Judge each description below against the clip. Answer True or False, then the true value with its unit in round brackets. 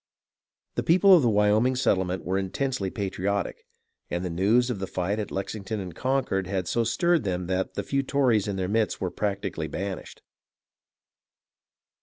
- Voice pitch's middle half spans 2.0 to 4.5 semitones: True (4.2 semitones)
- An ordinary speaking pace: True (170 wpm)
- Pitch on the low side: True (100 Hz)